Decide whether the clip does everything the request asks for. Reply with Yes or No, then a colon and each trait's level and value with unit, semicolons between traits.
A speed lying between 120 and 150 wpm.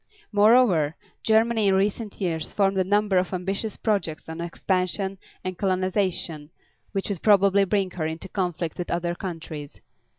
Yes: average, 145 wpm